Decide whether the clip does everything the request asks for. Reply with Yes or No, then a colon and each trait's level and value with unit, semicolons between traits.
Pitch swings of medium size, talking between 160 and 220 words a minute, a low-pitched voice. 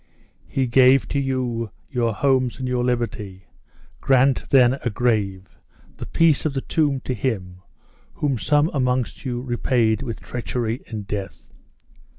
No: average, 3.1 semitones; average, 145 wpm; low, 125 Hz